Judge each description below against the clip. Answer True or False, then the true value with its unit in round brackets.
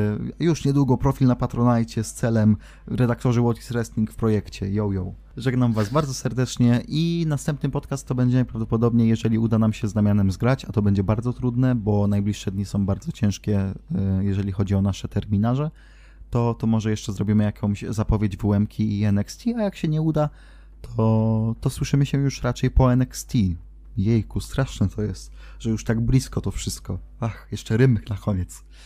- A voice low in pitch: True (110 Hz)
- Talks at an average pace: False (180 wpm)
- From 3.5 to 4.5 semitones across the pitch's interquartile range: True (3.8 semitones)